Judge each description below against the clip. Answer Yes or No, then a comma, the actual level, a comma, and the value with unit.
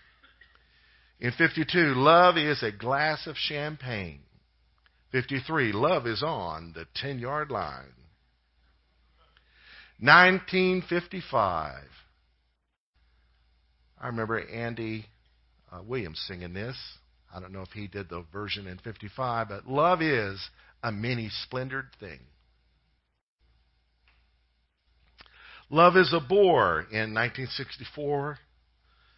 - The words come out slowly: Yes, slow, 95 wpm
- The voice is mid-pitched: No, low, 100 Hz